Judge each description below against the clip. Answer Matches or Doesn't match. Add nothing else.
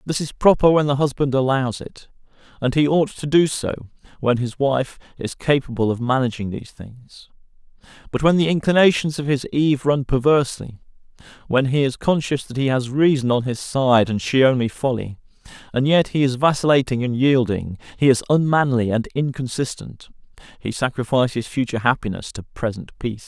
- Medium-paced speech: Matches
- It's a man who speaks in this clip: Matches